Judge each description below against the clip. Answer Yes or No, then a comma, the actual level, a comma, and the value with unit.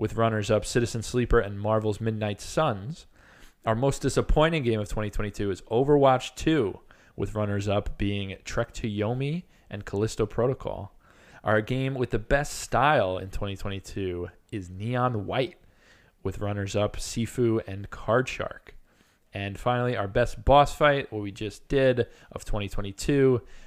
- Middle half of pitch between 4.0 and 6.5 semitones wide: No, average, 3.6 semitones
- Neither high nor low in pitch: No, low, 110 Hz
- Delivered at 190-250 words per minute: No, average, 145 wpm